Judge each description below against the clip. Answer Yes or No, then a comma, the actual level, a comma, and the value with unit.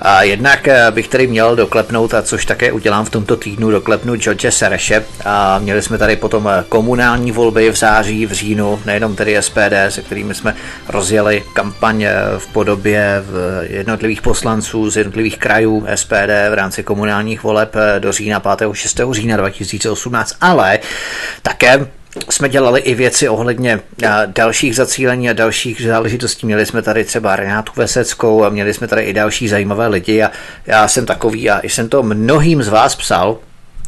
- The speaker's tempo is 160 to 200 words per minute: Yes, average, 165 wpm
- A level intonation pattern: Yes, narrow, 1.6 semitones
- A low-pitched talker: Yes, low, 110 Hz